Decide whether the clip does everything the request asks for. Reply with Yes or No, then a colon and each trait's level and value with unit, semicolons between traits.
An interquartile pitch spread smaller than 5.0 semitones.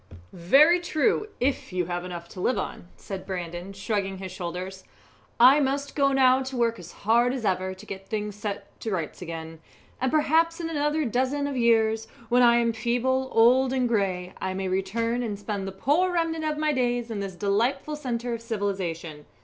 No: wide, 5.6 semitones